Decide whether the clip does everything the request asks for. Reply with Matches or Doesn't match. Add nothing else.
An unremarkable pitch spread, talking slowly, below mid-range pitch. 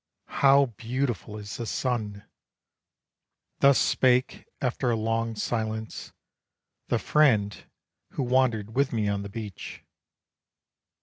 Matches